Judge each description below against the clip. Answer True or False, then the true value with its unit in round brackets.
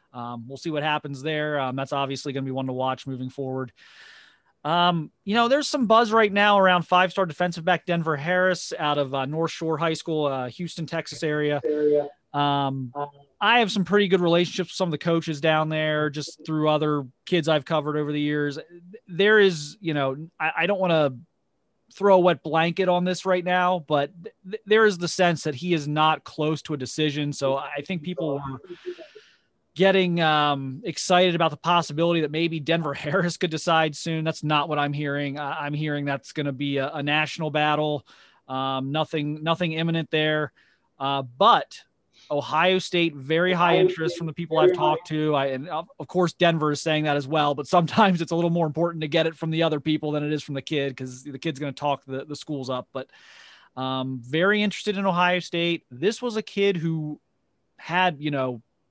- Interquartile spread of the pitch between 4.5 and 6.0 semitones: False (3.3 semitones)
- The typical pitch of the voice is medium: True (155 Hz)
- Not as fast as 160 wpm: False (205 wpm)